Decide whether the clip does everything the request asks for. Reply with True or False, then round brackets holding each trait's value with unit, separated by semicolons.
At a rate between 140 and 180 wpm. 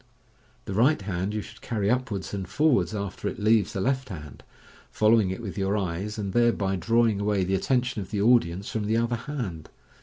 False (195 wpm)